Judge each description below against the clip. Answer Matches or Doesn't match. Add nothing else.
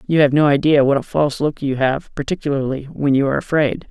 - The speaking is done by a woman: Doesn't match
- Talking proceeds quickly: Matches